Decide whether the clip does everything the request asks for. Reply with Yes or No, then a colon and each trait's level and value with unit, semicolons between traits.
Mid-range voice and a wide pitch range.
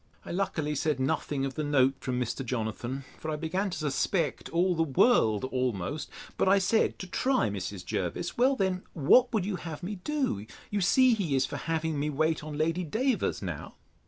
Yes: medium, 160 Hz; wide, 6.1 semitones